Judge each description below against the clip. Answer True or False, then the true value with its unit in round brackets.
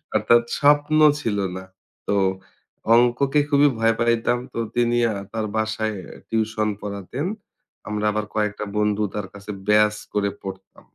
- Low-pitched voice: True (110 Hz)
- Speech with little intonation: True (2.3 semitones)